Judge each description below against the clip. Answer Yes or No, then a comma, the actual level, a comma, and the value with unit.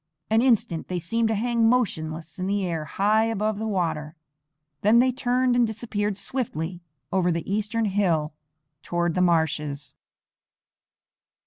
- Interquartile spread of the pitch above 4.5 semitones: Yes, average, 5.1 semitones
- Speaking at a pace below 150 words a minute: Yes, average, 140 wpm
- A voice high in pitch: Yes, high, 200 Hz